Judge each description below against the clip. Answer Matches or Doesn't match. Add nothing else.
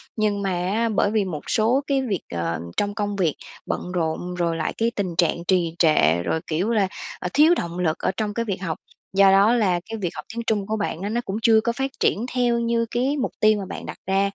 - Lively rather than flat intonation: Doesn't match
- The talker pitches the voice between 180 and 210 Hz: Matches